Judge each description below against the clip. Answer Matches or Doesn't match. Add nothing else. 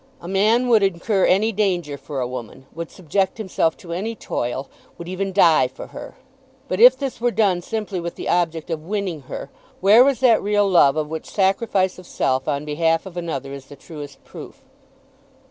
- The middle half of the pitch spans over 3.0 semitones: Matches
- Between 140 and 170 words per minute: Doesn't match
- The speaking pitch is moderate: Matches